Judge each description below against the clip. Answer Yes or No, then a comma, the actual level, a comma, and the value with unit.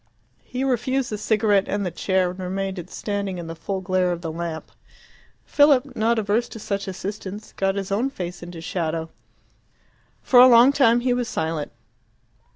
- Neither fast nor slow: Yes, average, 170 wpm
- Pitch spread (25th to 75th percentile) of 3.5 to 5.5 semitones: Yes, average, 4.7 semitones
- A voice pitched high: Yes, high, 200 Hz